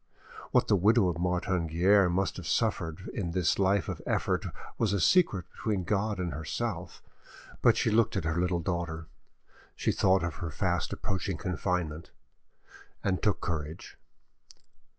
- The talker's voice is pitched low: Yes, very low, 90 Hz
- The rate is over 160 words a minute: No, average, 150 wpm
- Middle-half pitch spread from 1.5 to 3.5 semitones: Yes, average, 2.8 semitones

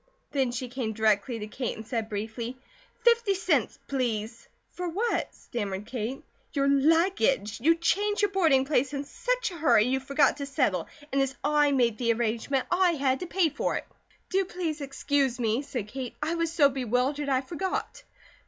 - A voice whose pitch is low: No, very high, 270 Hz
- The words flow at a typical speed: Yes, average, 175 wpm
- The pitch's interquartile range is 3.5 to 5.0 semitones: No, wide, 5.6 semitones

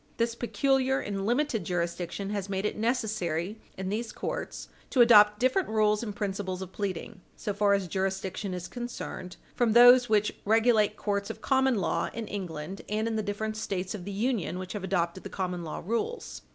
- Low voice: No, high, 205 Hz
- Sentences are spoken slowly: No, average, 185 wpm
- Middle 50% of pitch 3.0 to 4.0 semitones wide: Yes, average, 3.3 semitones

